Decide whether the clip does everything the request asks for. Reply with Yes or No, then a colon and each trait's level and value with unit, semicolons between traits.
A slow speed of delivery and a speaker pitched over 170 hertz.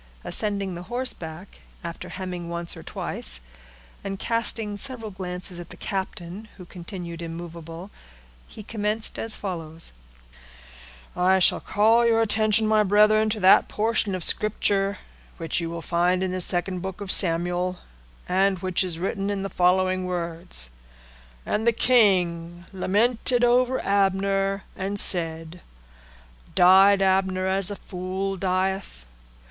Yes: slow, 130 wpm; high, 190 Hz